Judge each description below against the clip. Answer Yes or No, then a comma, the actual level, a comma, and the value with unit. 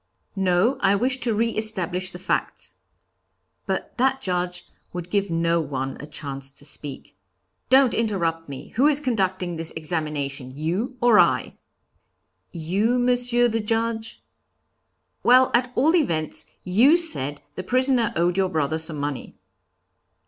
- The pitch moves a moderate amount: No, wide, 7.0 semitones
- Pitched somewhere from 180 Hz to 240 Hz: Yes, medium, 185 Hz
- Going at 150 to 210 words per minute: No, average, 140 wpm